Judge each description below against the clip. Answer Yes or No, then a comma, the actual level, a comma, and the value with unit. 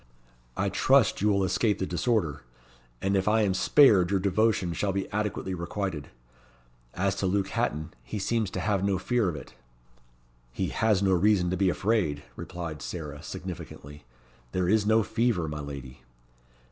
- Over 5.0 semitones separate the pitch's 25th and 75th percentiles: No, average, 3.5 semitones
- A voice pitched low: Yes, very low, 95 Hz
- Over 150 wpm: Yes, average, 165 wpm